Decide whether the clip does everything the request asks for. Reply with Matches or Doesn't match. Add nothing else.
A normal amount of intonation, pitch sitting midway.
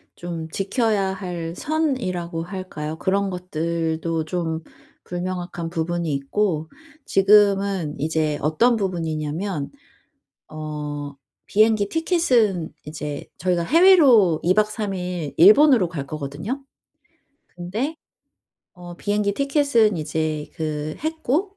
Matches